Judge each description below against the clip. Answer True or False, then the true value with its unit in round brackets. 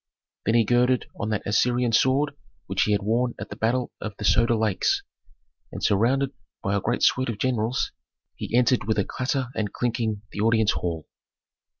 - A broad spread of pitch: False (3.0 semitones)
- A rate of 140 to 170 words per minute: False (185 wpm)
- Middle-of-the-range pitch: False (115 Hz)